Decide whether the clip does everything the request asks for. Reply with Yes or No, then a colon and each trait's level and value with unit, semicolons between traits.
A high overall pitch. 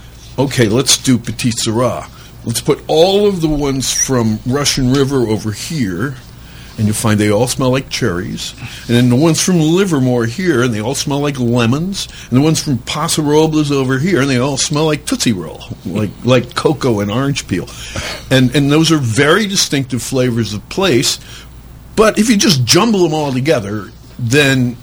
No: low, 130 Hz